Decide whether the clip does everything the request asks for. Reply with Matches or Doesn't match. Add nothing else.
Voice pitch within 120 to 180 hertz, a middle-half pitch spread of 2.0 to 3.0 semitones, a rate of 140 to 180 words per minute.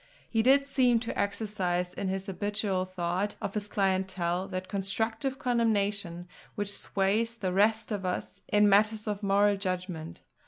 Doesn't match